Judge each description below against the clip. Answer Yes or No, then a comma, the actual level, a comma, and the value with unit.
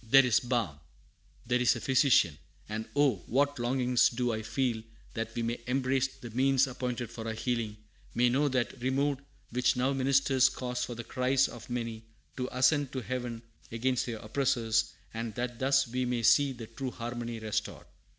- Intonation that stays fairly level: Yes, narrow, 2.3 semitones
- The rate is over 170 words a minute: Yes, average, 180 wpm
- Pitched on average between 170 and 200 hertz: No, low, 125 Hz